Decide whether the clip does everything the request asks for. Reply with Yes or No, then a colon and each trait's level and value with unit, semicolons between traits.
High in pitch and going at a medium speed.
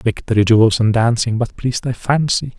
No: low, 115 Hz; average, 185 wpm